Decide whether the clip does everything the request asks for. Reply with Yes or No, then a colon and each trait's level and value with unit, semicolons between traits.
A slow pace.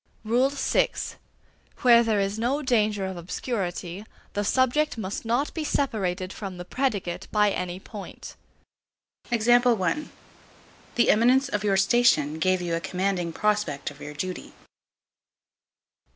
Yes: slow, 125 wpm